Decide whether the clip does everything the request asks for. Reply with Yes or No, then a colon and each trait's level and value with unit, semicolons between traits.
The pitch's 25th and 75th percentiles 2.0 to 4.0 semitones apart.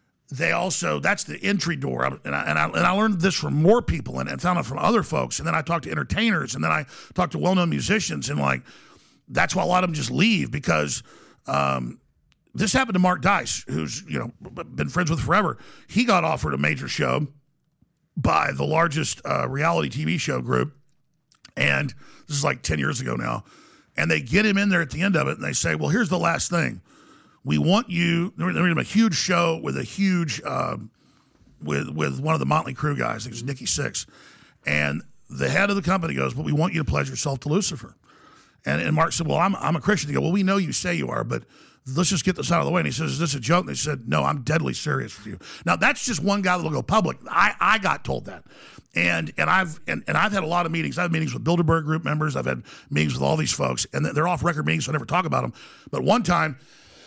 No: average, 4.9 semitones